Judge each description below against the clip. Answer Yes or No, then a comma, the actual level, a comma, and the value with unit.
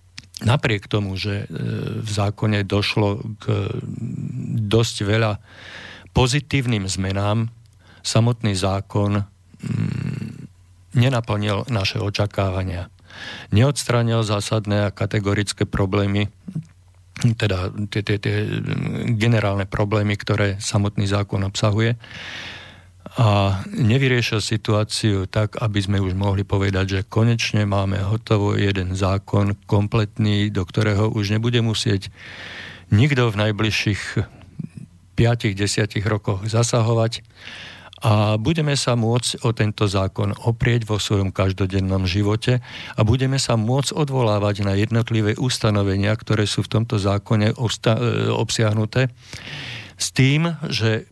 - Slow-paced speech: Yes, slow, 100 wpm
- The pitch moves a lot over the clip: No, narrow, 2.5 semitones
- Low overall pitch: Yes, low, 105 Hz